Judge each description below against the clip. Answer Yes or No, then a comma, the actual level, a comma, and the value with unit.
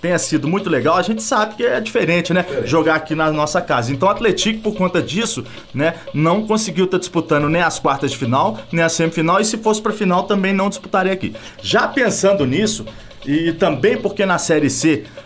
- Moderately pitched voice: Yes, medium, 175 Hz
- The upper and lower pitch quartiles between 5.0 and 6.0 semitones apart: No, average, 4.4 semitones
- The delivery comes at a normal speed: No, fast, 210 wpm